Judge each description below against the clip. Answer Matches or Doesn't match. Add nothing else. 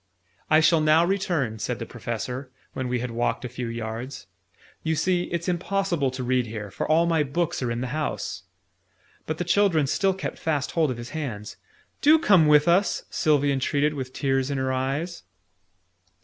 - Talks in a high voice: Doesn't match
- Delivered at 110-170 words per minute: Doesn't match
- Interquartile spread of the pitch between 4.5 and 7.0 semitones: Matches